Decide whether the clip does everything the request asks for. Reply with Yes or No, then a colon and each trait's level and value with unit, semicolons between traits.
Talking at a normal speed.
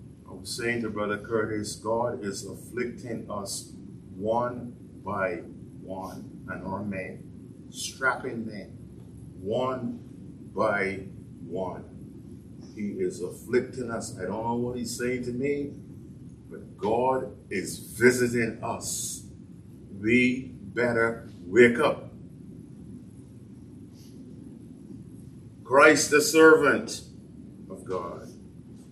No: slow, 95 wpm